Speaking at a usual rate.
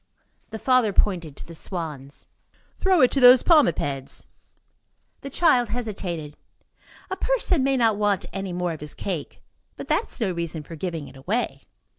Yes: average, 165 wpm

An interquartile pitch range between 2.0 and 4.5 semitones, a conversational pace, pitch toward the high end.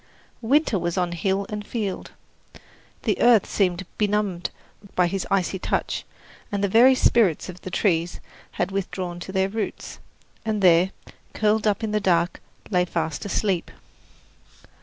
Yes: average, 3.0 semitones; average, 145 wpm; high, 195 Hz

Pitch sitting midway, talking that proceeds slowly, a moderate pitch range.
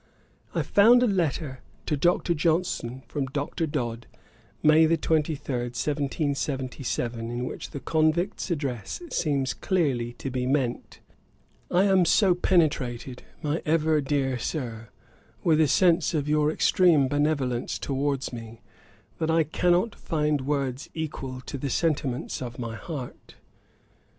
Yes: medium, 145 Hz; slow, 130 wpm; average, 4.1 semitones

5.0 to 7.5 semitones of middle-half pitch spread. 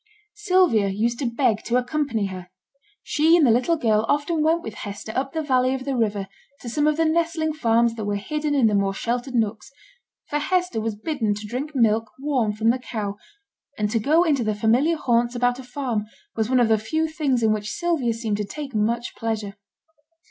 Yes: wide, 5.4 semitones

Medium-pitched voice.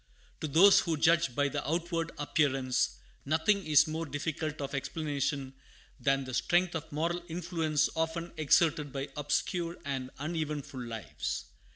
Yes: medium, 155 Hz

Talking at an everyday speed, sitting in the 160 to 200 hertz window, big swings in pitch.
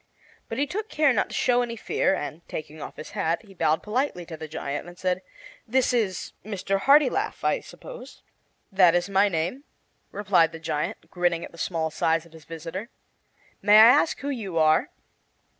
Yes: average, 190 wpm; medium, 185 Hz; wide, 6.5 semitones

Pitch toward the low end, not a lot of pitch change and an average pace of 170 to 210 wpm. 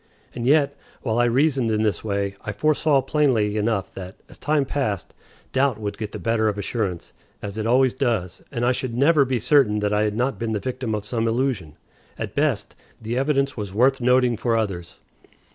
No: low, 115 Hz; average, 4.0 semitones; average, 200 wpm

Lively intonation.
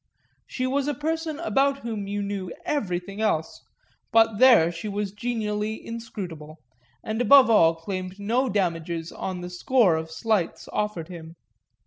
No: average, 5.0 semitones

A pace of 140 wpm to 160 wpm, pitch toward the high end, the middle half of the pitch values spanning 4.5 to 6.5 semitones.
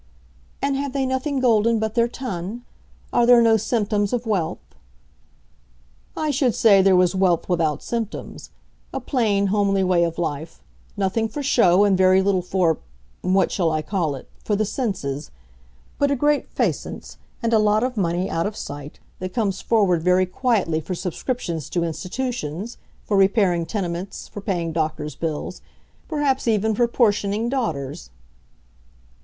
Yes: average, 150 wpm; high, 195 Hz; average, 5.2 semitones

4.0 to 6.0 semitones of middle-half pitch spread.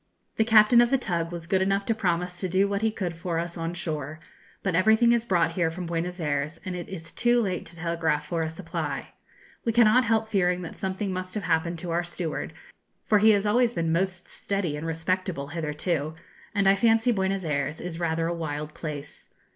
No: average, 3.4 semitones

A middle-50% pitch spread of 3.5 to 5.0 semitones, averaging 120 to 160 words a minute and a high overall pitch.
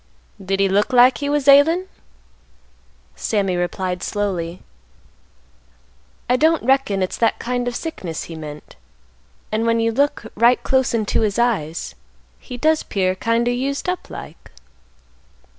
No: wide, 5.4 semitones; average, 140 wpm; high, 230 Hz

